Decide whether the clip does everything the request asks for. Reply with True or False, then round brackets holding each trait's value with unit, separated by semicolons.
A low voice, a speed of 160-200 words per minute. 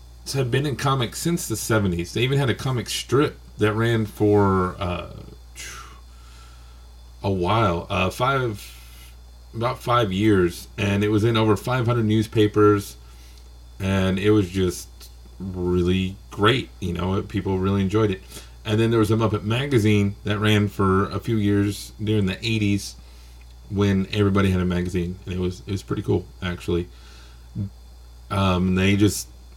False (95 Hz; 150 wpm)